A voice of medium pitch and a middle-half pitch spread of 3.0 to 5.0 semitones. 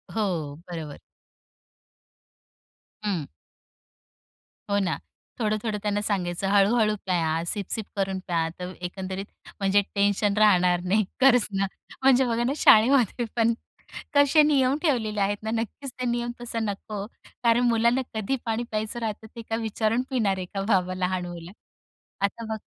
No: high, 215 Hz; average, 3.5 semitones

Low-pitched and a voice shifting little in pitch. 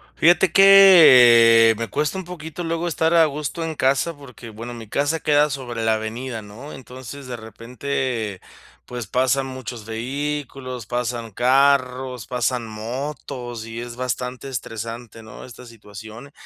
No: low, 125 Hz; average, 3.6 semitones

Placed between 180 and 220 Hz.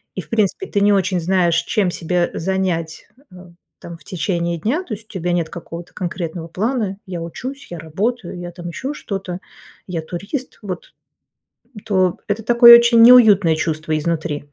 Yes: medium, 185 Hz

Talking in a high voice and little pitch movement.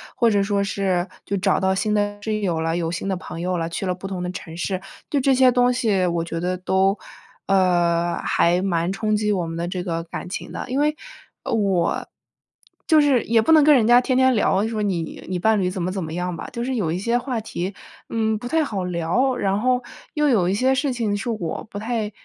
No: high, 200 Hz; average, 4.7 semitones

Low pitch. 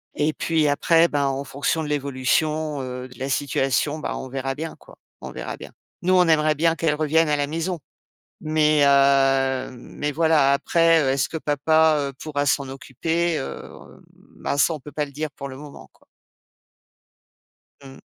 No: medium, 145 Hz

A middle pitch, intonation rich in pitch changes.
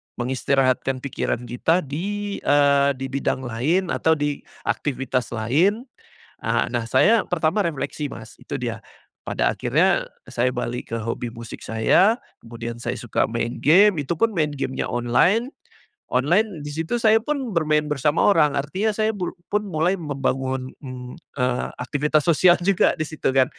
Yes: medium, 145 Hz; wide, 5.8 semitones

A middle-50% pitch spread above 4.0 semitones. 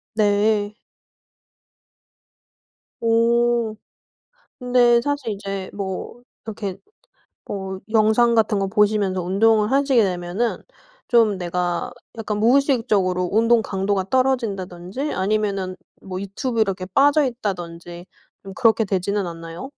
No: average, 3.7 semitones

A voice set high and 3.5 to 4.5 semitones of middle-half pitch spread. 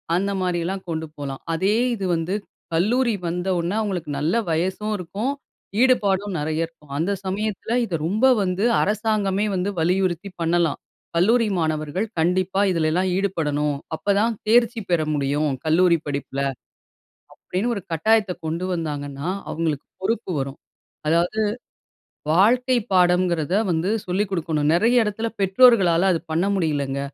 No: medium, 180 Hz; average, 4.0 semitones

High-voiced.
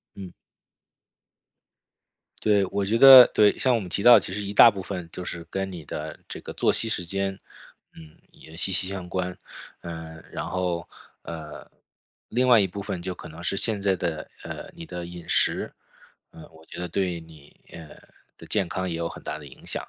No: very low, 90 Hz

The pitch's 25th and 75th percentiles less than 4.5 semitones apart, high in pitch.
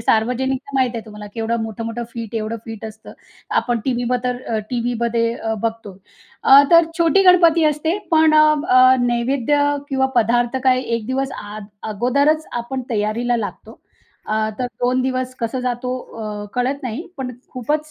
Yes: average, 2.8 semitones; high, 245 Hz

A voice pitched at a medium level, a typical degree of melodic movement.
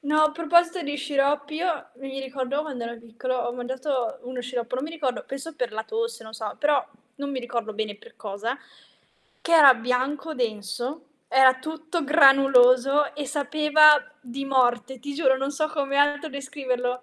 No: very high, 270 Hz; average, 3.1 semitones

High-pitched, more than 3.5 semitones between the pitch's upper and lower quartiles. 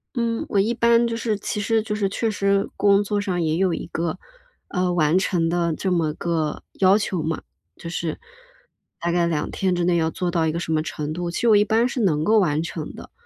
No: medium, 180 Hz; average, 3.9 semitones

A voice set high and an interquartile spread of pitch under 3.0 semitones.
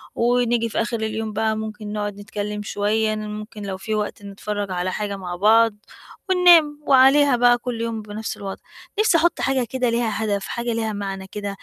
Yes: high, 220 Hz; narrow, 2.6 semitones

